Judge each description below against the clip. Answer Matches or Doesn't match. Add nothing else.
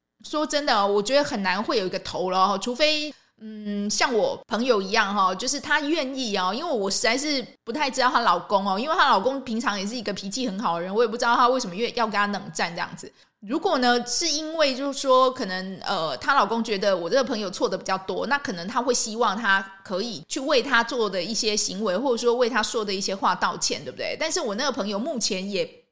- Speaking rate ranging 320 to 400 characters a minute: Matches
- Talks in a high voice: Matches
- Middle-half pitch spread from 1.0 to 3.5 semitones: Doesn't match